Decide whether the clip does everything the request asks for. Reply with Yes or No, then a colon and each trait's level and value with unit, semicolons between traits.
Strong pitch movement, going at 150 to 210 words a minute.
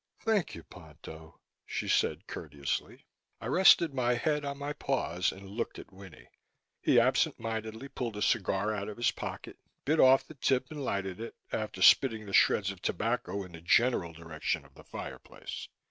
Yes: wide, 6.0 semitones; average, 175 wpm